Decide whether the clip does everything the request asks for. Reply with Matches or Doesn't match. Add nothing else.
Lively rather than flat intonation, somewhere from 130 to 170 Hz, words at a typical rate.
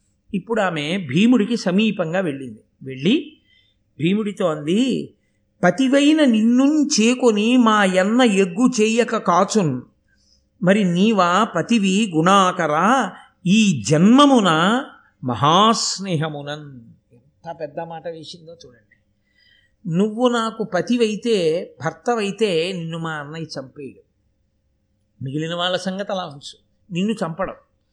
Doesn't match